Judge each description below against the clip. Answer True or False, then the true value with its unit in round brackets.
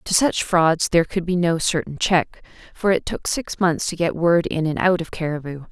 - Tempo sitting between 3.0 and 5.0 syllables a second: True (4.9 syllables/s)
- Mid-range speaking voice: True (170 Hz)